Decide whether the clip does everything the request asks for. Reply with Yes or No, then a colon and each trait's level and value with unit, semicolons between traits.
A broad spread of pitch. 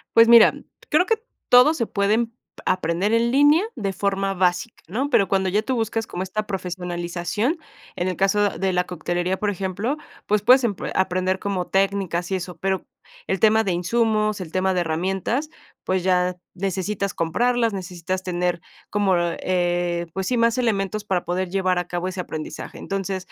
No: average, 3.0 semitones